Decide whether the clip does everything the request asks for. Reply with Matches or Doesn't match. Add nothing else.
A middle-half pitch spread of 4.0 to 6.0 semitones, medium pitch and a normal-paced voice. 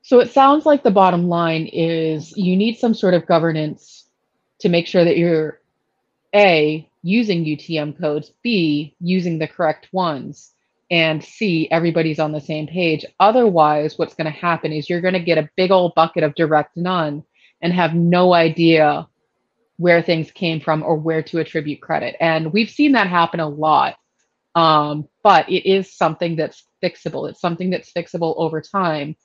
Doesn't match